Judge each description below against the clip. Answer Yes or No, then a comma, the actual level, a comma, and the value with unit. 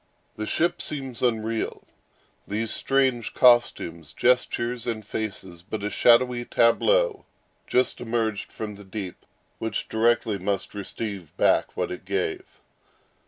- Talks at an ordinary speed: No, slow, 120 wpm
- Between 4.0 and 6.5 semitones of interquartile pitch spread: No, average, 3.1 semitones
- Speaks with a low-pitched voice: Yes, low, 110 Hz